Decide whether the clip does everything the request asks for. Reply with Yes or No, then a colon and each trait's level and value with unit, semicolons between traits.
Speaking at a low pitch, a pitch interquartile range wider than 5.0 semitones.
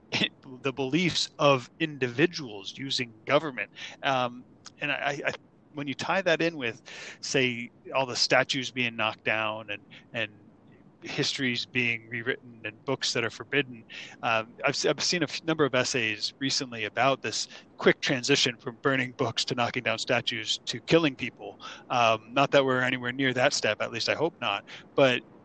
No: low, 130 Hz; average, 2.9 semitones